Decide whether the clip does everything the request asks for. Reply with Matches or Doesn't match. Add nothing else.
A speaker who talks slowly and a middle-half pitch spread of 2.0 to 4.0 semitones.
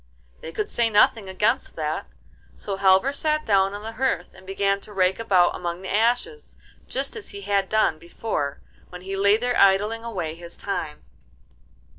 Doesn't match